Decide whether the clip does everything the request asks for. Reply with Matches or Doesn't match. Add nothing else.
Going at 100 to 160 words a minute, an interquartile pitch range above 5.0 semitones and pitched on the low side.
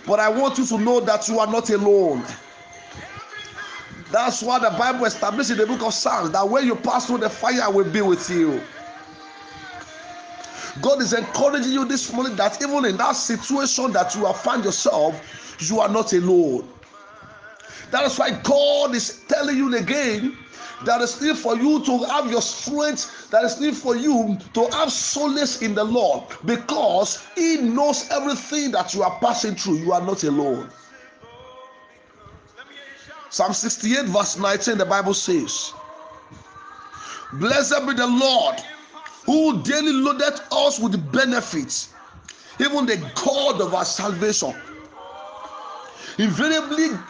Doesn't match